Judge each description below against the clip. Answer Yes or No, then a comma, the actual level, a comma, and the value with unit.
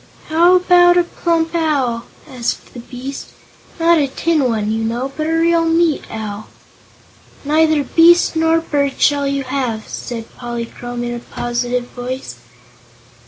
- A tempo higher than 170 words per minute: No, average, 145 wpm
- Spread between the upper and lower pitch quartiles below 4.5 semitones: No, average, 5.3 semitones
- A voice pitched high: Yes, very high, 280 Hz